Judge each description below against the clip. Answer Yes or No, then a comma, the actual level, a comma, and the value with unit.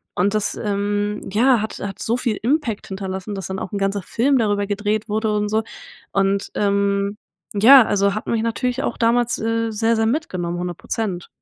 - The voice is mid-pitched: No, high, 210 Hz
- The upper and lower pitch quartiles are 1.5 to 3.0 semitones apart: Yes, narrow, 2.4 semitones